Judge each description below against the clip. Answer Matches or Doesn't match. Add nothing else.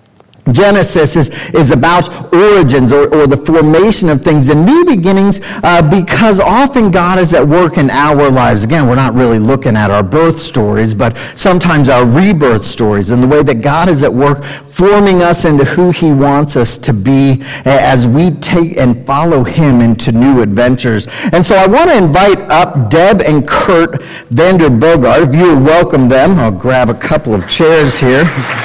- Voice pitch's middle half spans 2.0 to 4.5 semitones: Doesn't match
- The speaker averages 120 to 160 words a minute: Doesn't match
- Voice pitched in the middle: Matches